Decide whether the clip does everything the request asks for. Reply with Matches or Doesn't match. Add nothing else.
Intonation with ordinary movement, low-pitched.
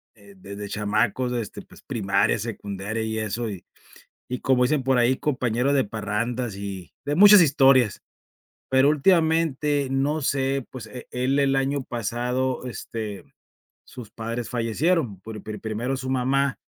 Matches